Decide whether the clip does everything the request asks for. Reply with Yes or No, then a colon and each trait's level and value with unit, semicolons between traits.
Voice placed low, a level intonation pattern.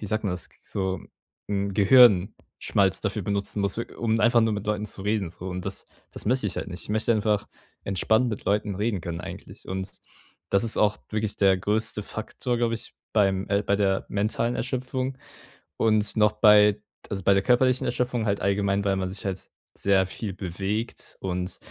Yes: low, 105 Hz; narrow, 2.2 semitones